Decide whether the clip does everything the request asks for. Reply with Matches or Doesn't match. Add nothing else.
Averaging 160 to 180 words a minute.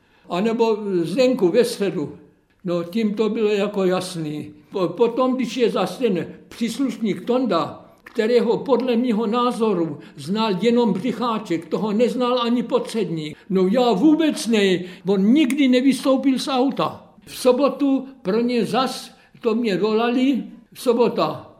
Doesn't match